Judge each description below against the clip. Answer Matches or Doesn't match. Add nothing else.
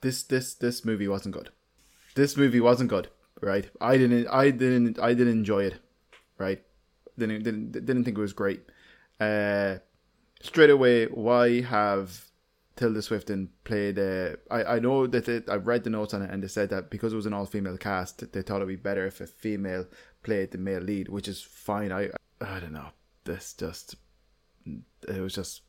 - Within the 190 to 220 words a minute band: Matches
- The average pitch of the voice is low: Matches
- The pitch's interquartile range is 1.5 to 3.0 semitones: Doesn't match